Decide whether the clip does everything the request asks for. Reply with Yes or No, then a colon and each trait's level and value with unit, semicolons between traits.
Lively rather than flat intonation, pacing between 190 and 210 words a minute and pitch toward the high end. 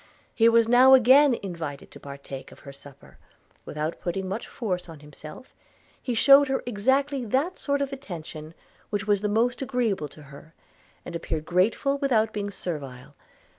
No: wide, 8.5 semitones; average, 165 wpm; high, 205 Hz